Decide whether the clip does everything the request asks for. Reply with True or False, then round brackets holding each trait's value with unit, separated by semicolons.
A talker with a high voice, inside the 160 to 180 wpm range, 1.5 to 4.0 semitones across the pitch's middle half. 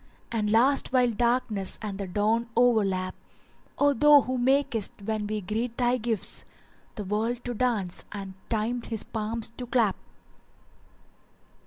False (225 Hz; 150 wpm; 2.8 semitones)